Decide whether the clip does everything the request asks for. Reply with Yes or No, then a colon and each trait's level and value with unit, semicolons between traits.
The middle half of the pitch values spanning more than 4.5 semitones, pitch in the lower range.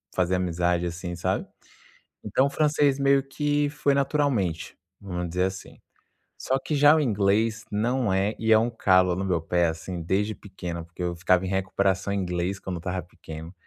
Yes: wide, 5.4 semitones; very low, 95 Hz